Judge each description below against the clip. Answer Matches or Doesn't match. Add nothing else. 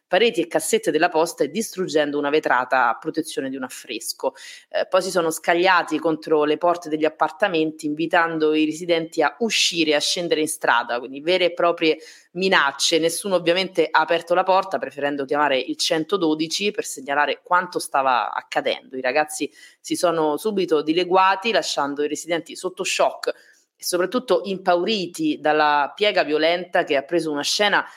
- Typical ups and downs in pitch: Matches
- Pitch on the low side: Doesn't match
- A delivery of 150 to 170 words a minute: Matches